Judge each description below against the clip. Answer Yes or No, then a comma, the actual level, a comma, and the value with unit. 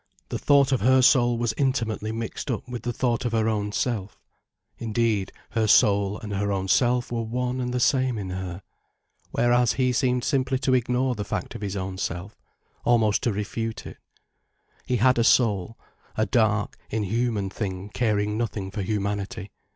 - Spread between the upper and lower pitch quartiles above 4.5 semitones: No, average, 3.3 semitones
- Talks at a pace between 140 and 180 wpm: Yes, average, 175 wpm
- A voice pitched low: Yes, low, 115 Hz